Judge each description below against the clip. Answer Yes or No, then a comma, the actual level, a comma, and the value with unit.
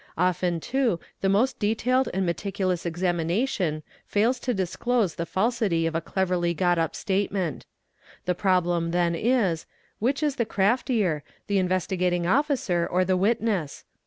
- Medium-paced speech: Yes, average, 150 wpm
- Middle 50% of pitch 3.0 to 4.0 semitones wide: No, average, 4.6 semitones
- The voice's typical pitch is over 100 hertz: Yes, medium, 185 Hz